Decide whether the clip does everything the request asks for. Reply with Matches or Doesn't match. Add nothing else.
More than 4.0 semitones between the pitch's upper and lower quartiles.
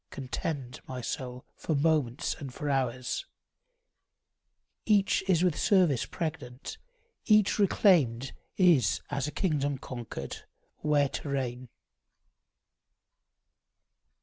Matches